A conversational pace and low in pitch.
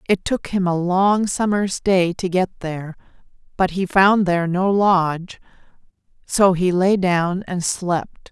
No: average, 160 wpm; medium, 185 Hz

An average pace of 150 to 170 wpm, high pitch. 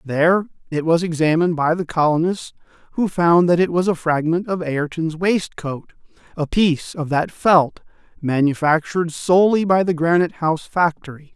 No: average, 155 wpm; medium, 165 Hz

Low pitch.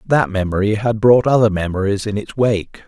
Yes: low, 105 Hz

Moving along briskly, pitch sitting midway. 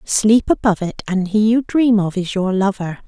No: fast, 215 wpm; high, 205 Hz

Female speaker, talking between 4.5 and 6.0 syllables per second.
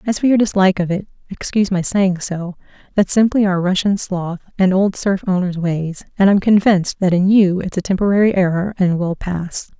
Yes: female; 5.4 syllables/s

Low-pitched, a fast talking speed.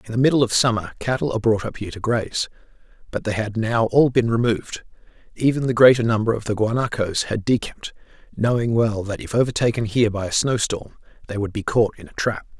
Yes: low, 115 Hz; fast, 215 wpm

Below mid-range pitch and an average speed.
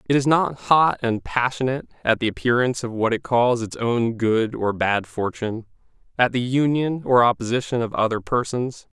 Yes: low, 120 Hz; average, 180 wpm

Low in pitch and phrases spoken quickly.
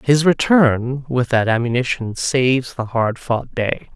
No: low, 125 Hz; average, 150 wpm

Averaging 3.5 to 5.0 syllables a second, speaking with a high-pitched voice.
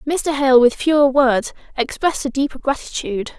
No: 5.4 syllables/s; very high, 270 Hz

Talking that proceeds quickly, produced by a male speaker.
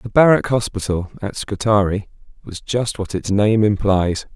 No: average, 150 wpm; male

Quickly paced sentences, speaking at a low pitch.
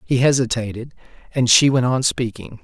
No: slow, 135 wpm; low, 125 Hz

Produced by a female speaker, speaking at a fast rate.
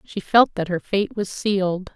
Yes: female; fast, 215 wpm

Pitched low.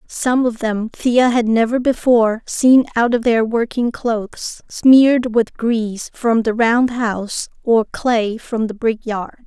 No: high, 230 Hz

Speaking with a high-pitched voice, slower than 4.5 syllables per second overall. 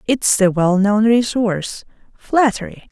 Yes: high, 210 Hz; 4.0 syllables/s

